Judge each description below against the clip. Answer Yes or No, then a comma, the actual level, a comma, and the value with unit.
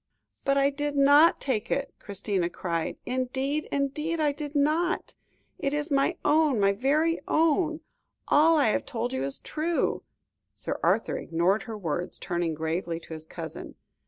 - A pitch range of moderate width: No, wide, 7.4 semitones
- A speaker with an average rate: Yes, average, 160 wpm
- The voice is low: No, very high, 275 Hz